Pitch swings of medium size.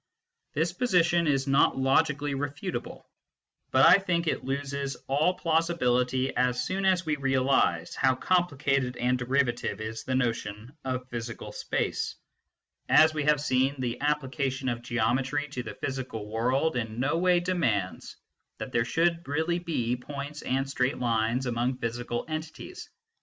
Yes: average, 4.1 semitones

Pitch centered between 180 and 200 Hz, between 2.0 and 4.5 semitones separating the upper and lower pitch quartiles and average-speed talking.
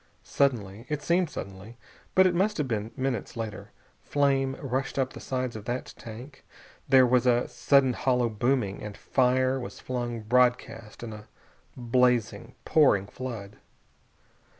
No: low, 125 Hz; average, 2.9 semitones; average, 145 wpm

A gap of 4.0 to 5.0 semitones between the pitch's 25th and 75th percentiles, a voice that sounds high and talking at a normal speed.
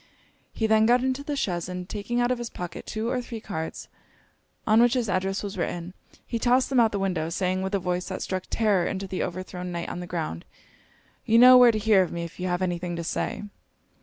No: average, 4.4 semitones; high, 195 Hz; fast, 245 wpm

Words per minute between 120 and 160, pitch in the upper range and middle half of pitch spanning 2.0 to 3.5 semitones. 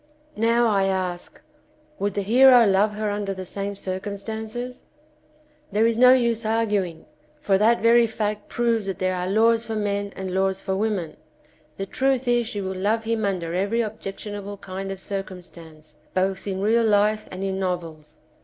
No: average, 170 wpm; high, 205 Hz; average, 2.8 semitones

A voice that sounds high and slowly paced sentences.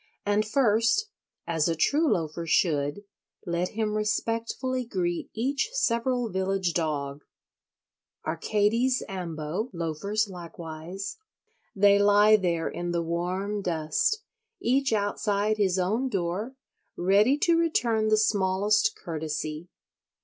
Yes: high, 200 Hz; slow, 105 wpm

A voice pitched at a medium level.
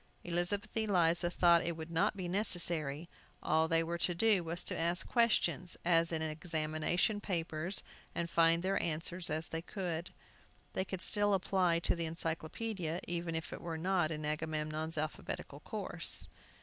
Yes: medium, 170 Hz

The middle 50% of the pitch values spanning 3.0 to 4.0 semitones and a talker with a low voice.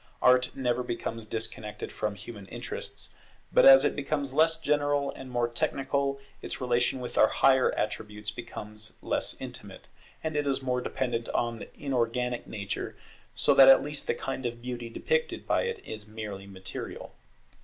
Yes: average, 3.7 semitones; low, 125 Hz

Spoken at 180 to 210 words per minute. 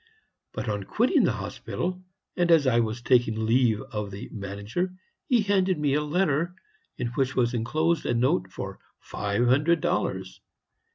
No: average, 160 wpm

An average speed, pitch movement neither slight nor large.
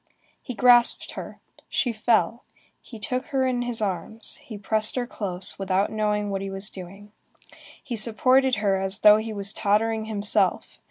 Yes: average, 160 wpm; average, 3.2 semitones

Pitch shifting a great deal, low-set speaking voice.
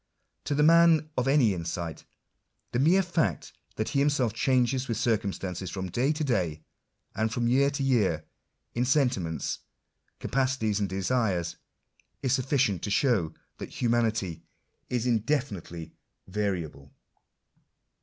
Yes: wide, 6.2 semitones; low, 115 Hz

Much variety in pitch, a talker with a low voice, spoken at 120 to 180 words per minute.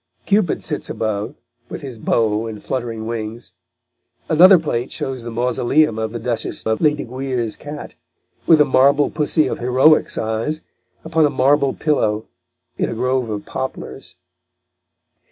No: average, 4.6 semitones; low, 125 Hz; average, 140 wpm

